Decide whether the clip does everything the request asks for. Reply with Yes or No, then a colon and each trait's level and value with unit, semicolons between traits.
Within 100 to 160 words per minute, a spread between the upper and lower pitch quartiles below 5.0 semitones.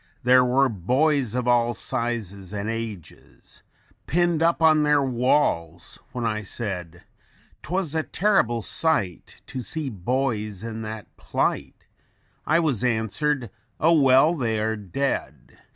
No: slow, 135 wpm; wide, 5.5 semitones